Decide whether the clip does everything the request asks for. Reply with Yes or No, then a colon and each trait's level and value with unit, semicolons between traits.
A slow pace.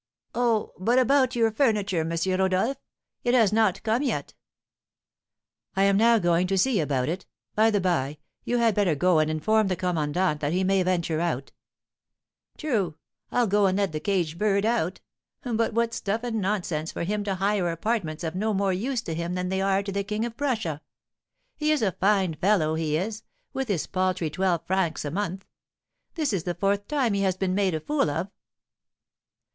No: average, 195 wpm